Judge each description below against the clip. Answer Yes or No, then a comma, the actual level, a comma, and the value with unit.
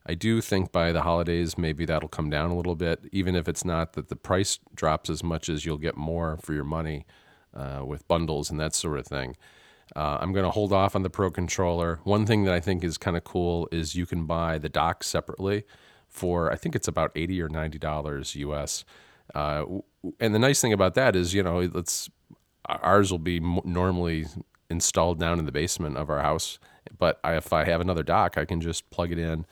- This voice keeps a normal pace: No, fast, 220 wpm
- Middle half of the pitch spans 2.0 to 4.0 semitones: Yes, narrow, 2.4 semitones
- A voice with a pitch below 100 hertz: Yes, very low, 85 Hz